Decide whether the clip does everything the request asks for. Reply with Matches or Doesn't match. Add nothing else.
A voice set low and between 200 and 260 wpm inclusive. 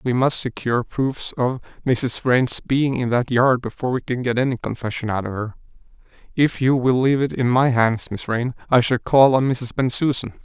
Matches